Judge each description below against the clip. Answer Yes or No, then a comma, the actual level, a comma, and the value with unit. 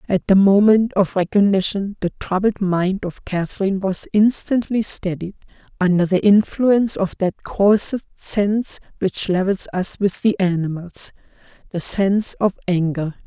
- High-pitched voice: Yes, high, 195 Hz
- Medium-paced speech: No, slow, 130 wpm